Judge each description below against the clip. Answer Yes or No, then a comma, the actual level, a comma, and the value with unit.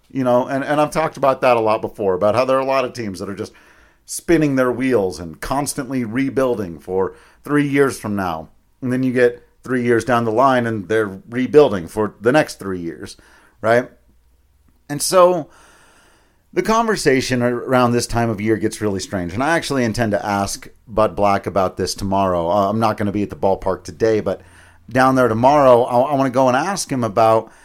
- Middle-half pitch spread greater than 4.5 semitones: Yes, average, 4.9 semitones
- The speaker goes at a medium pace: No, fast, 210 wpm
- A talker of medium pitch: No, low, 120 Hz